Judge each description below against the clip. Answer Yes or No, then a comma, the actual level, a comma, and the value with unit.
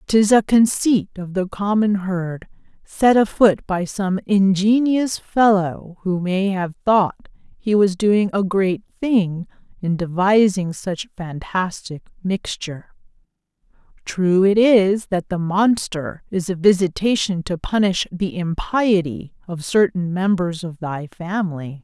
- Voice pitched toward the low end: No, high, 190 Hz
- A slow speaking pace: Yes, slow, 130 wpm